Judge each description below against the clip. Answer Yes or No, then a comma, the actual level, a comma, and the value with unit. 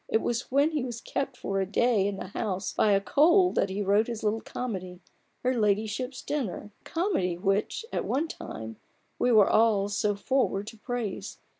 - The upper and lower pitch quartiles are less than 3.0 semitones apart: No, average, 4.3 semitones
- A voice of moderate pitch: No, high, 215 Hz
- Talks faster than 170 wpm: Yes, average, 195 wpm